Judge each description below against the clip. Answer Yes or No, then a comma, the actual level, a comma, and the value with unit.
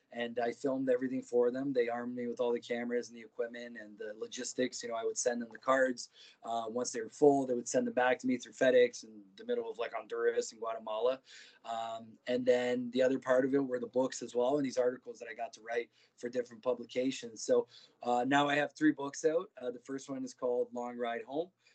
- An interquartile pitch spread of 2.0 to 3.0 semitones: Yes, average, 2.7 semitones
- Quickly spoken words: Yes, fast, 250 wpm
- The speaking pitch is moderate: No, low, 125 Hz